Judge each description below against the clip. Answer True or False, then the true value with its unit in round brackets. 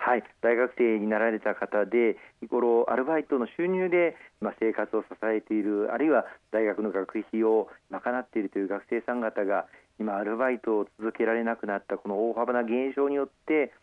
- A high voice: False (110 Hz)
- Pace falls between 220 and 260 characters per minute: False (355 characters per minute)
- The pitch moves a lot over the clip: False (2.5 semitones)